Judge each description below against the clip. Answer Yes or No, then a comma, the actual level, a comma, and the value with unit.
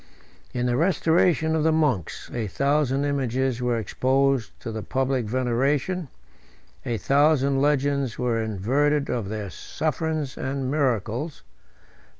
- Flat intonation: No, average, 3.4 semitones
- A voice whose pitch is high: No, low, 135 Hz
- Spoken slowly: Yes, slow, 125 wpm